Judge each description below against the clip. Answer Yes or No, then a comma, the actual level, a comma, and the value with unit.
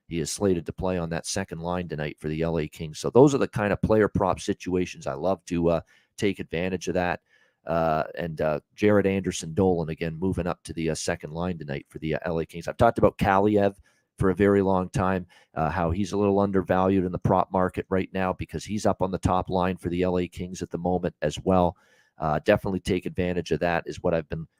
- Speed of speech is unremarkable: No, fast, 240 wpm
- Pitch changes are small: Yes, narrow, 2.2 semitones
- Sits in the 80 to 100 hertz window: Yes, very low, 90 Hz